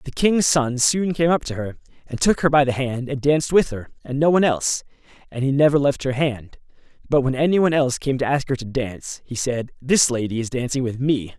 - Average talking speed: No, fast, 245 wpm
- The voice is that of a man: Yes, male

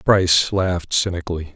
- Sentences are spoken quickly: No, slow, 115 wpm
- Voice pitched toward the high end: No, very low, 90 Hz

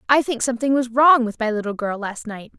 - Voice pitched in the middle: No, high, 240 Hz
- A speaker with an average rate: No, fast, 255 wpm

